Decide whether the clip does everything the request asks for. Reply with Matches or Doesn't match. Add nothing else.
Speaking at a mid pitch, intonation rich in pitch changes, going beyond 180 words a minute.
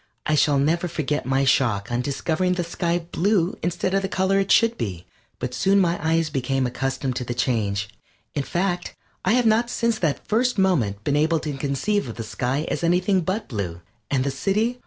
Matches